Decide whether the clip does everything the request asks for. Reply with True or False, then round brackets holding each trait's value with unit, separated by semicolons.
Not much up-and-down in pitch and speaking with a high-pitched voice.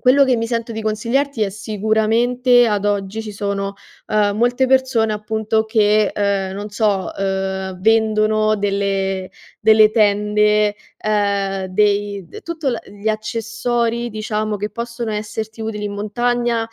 True (2.0 semitones; 215 Hz)